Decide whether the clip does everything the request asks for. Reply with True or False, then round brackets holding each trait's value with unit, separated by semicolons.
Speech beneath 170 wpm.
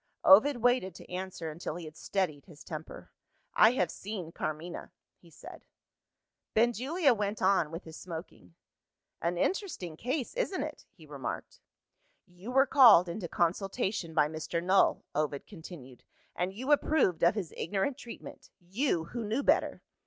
True (150 wpm)